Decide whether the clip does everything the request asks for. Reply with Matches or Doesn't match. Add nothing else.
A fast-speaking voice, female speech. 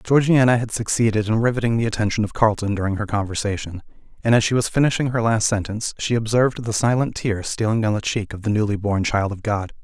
Doesn't match